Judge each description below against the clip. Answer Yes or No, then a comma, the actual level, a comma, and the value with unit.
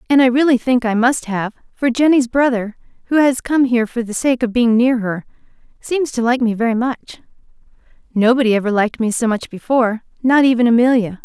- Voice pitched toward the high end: Yes, high, 240 Hz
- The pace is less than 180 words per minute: No, average, 200 wpm